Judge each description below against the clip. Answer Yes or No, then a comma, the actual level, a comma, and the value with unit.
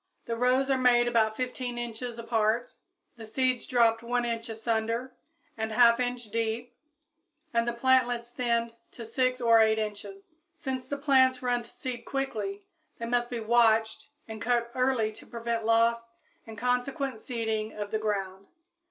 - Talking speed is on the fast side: No, average, 160 wpm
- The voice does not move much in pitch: Yes, narrow, 1.9 semitones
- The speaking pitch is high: Yes, high, 235 Hz